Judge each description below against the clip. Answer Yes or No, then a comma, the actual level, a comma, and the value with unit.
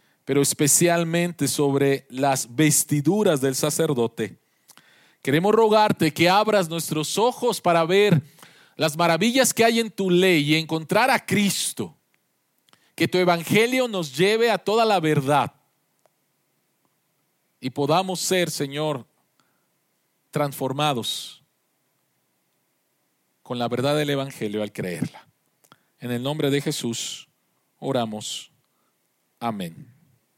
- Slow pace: Yes, slow, 105 wpm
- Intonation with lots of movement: No, average, 4.8 semitones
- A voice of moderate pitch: Yes, medium, 155 Hz